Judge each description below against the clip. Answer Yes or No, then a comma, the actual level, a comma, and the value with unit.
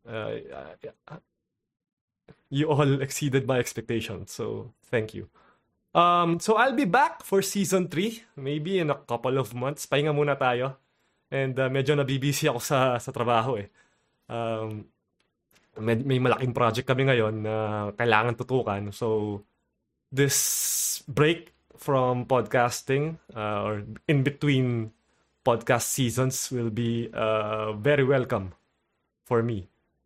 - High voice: No, low, 130 Hz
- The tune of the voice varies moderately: Yes, average, 3.7 semitones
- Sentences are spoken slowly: No, average, 125 wpm